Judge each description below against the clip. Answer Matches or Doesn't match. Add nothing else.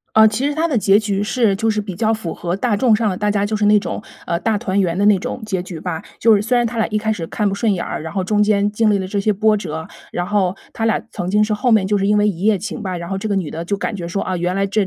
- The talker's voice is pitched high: Matches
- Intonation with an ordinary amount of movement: Doesn't match